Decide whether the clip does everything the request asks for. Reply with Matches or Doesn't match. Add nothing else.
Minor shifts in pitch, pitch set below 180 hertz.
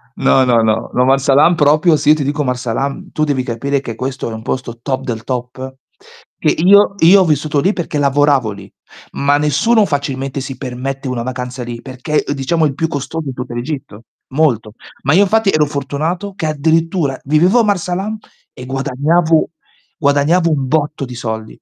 Doesn't match